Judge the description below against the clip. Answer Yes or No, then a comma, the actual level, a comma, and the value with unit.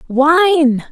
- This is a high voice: Yes, very high, 300 Hz